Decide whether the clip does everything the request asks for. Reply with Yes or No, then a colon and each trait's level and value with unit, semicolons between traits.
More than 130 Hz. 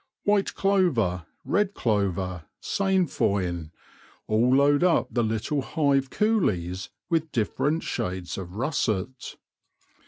No: low, 125 Hz